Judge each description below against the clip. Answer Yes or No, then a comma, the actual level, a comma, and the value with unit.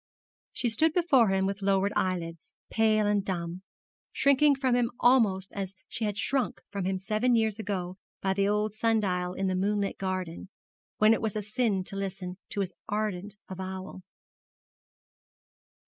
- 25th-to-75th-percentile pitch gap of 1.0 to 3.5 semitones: Yes, average, 2.7 semitones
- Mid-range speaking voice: No, high, 200 Hz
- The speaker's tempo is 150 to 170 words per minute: Yes, average, 160 wpm